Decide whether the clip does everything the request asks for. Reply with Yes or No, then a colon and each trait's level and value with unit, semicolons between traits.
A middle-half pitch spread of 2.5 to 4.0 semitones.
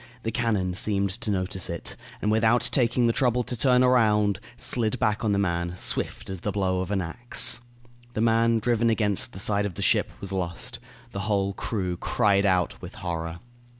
Yes: average, 3.6 semitones